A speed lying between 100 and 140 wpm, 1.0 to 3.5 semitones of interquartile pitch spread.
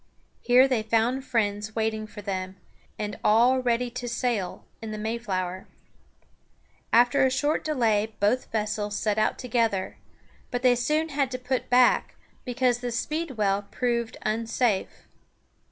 Yes: slow, 135 wpm; average, 3.0 semitones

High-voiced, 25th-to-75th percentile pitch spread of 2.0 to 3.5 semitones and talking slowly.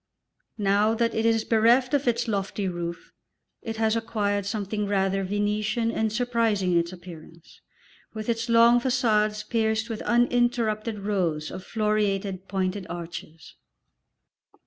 Yes: high, 215 Hz; average, 2.9 semitones; slow, 130 wpm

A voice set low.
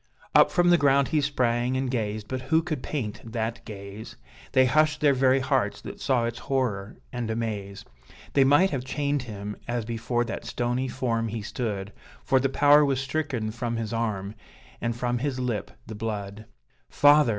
Yes: low, 120 Hz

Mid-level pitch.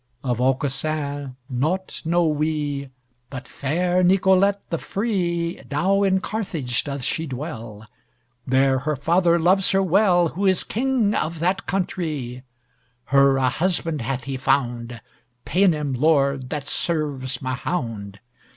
Yes: medium, 150 Hz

